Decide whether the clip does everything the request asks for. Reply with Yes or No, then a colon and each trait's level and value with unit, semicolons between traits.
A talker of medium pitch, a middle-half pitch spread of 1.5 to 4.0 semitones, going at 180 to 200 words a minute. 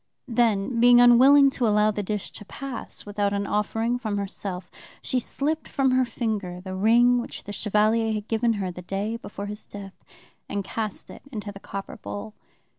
No: high, 215 Hz; average, 2.9 semitones; average, 185 wpm